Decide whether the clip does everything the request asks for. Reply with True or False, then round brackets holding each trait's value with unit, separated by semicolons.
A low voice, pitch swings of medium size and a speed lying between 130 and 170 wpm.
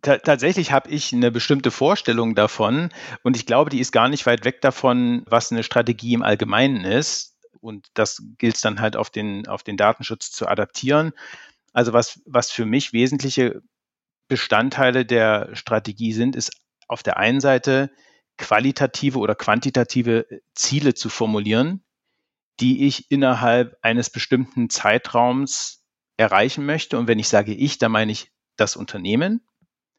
True (125 Hz; 3.2 semitones; 150 wpm)